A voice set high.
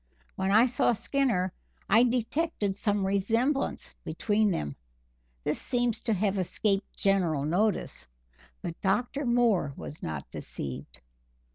Yes: high, 205 Hz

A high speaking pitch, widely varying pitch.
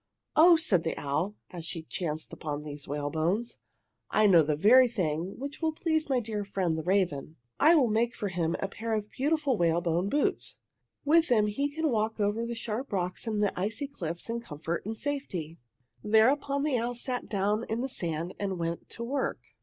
Yes: high, 210 Hz; wide, 6.8 semitones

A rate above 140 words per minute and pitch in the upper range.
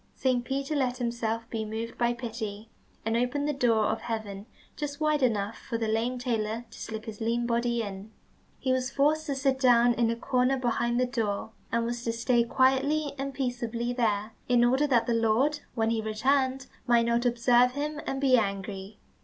Yes: average, 195 wpm; high, 240 Hz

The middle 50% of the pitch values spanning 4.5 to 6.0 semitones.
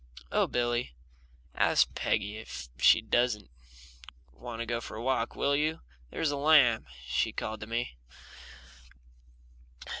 No: average, 3.2 semitones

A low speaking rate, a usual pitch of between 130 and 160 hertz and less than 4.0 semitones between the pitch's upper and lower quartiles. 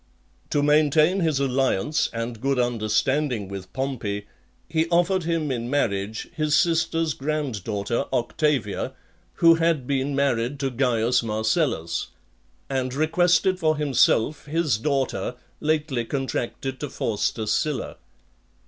No: slow, 120 wpm; low, 135 Hz; average, 4.8 semitones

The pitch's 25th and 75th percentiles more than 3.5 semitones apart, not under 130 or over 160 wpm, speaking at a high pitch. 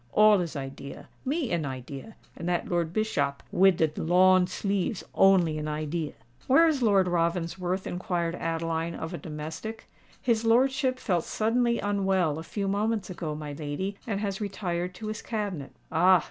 No: average, 4.5 semitones; average, 155 wpm; medium, 180 Hz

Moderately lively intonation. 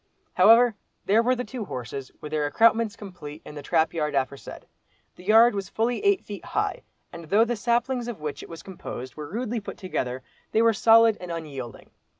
No: wide, 7.2 semitones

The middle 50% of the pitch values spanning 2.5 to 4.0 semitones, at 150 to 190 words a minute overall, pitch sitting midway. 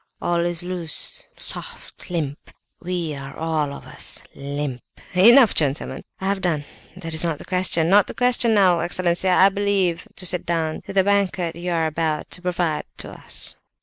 Yes: average, 2.8 semitones; average, 180 wpm; medium, 175 Hz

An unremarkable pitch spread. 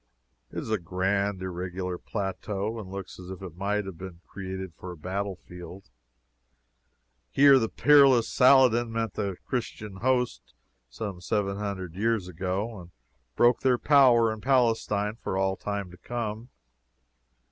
Yes: average, 3.5 semitones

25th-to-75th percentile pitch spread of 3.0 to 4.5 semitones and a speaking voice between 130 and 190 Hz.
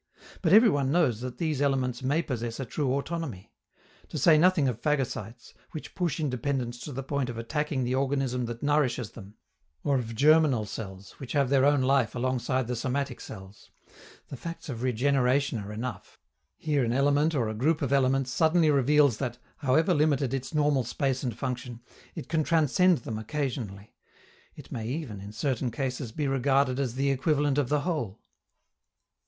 Yes: average, 3.4 semitones; low, 135 Hz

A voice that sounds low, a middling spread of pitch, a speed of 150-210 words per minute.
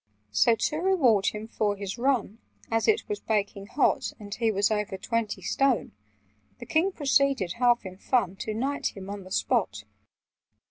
No: high, 225 Hz; average, 5.0 semitones; average, 170 wpm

